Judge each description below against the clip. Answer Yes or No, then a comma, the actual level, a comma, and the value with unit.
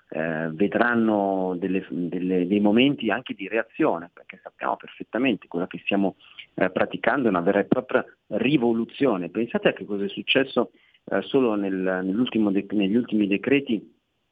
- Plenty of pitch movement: No, average, 3.3 semitones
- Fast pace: No, average, 155 wpm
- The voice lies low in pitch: Yes, low, 100 Hz